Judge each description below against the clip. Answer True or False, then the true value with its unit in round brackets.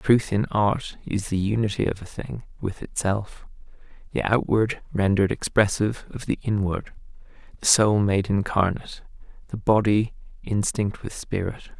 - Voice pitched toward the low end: True (105 Hz)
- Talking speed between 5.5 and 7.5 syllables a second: False (4.8 syllables/s)